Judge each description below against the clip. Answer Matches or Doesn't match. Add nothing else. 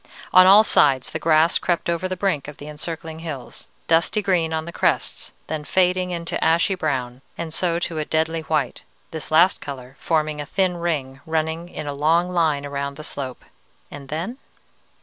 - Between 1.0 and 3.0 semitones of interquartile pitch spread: Matches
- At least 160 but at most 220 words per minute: Matches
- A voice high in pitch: Doesn't match